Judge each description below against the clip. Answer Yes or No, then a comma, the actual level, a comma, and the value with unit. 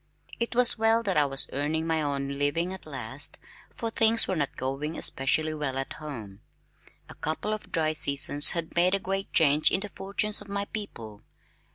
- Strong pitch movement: Yes, wide, 5.8 semitones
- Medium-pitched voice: Yes, medium, 160 Hz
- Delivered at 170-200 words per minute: Yes, average, 190 wpm